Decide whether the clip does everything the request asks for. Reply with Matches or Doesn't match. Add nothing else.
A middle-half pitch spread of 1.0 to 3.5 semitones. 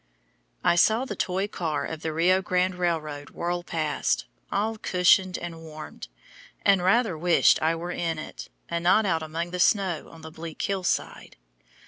Matches